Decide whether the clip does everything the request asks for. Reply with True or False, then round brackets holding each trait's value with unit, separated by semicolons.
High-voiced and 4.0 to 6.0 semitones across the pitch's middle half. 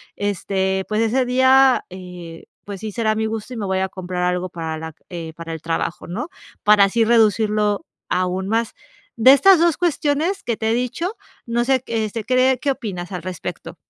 True (215 Hz; 5.4 semitones)